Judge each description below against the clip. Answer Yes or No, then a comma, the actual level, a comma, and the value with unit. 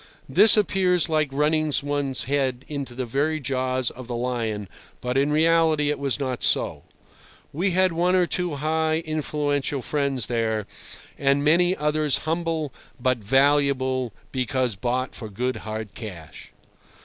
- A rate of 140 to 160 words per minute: Yes, average, 145 wpm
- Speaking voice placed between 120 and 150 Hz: Yes, medium, 140 Hz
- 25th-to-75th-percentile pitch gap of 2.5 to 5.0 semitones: Yes, average, 3.7 semitones